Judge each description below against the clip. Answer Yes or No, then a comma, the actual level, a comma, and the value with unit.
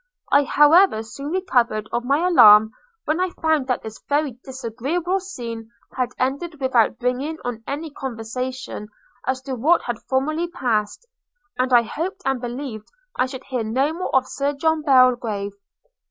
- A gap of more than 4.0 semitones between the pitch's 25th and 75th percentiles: Yes, average, 4.4 semitones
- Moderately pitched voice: No, very high, 260 Hz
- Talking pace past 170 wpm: No, average, 155 wpm